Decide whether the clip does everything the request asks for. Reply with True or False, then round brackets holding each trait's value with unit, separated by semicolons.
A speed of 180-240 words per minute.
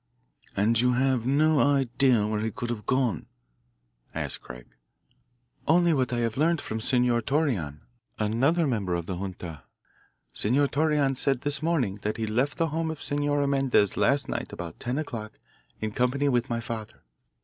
False (165 wpm)